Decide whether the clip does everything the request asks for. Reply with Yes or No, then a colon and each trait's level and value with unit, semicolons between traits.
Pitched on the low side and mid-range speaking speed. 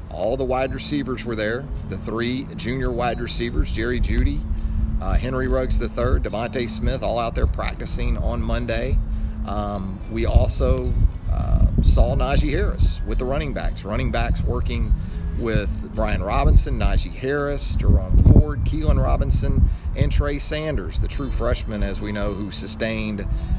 Yes: low, 105 Hz; average, 150 wpm